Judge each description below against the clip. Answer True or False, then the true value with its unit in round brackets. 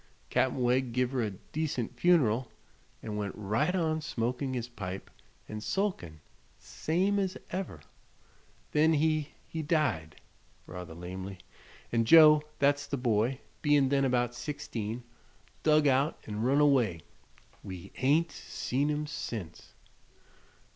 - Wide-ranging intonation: True (5.8 semitones)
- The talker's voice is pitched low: True (130 Hz)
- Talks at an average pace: False (125 wpm)